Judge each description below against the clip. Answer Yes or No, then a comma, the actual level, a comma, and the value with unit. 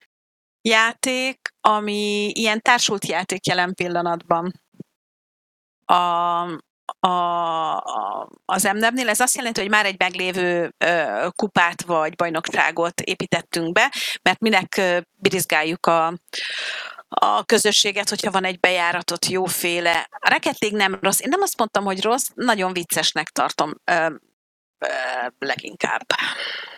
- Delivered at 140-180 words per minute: No, average, 120 wpm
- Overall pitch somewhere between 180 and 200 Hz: Yes, medium, 185 Hz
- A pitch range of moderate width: Yes, average, 3.8 semitones